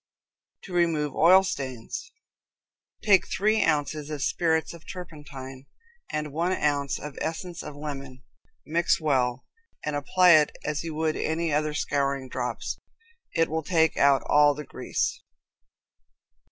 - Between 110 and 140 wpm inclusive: Yes, slow, 135 wpm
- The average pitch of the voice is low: No, medium, 150 Hz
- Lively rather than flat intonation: No, average, 2.9 semitones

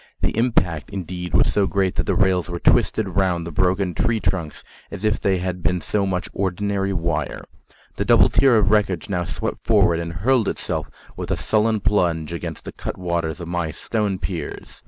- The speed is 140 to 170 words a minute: No, average, 190 wpm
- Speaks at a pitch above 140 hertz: No, very low, 90 Hz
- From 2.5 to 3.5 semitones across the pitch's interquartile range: Yes, average, 2.8 semitones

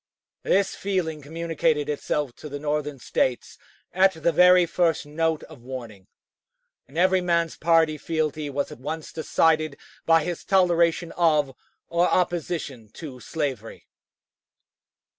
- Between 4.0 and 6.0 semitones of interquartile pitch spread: No, average, 2.8 semitones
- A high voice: No, medium, 160 Hz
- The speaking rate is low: Yes, slow, 125 wpm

